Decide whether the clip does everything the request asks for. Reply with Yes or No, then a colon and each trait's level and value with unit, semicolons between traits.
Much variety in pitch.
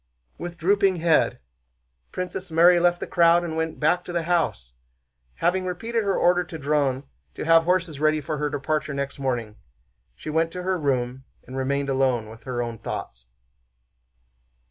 No: average, 4.5 semitones